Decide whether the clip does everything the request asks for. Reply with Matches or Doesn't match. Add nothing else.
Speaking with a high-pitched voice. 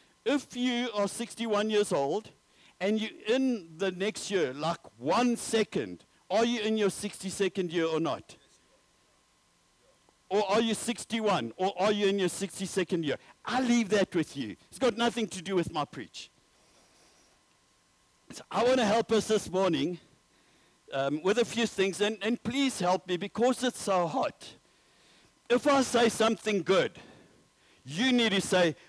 Matches